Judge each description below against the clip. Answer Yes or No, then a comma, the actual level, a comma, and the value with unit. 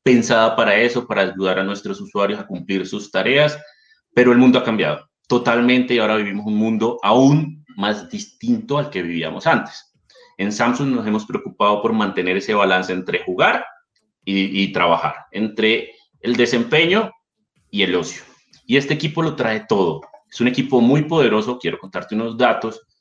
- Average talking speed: Yes, average, 170 wpm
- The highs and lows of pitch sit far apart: Yes, wide, 6.6 semitones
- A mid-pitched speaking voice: No, low, 120 Hz